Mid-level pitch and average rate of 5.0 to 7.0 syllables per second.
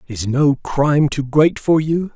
No: medium, 145 Hz; 4.0 syllables/s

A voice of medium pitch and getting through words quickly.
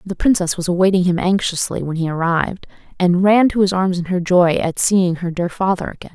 Yes: medium, 180 Hz; fast, 225 wpm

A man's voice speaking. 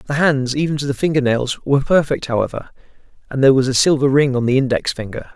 Yes: male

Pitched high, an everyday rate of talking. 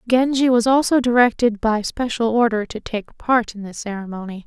Yes: high, 230 Hz; average, 175 wpm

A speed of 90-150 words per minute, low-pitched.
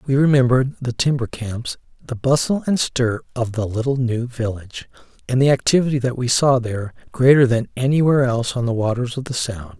No: average, 190 wpm; low, 125 Hz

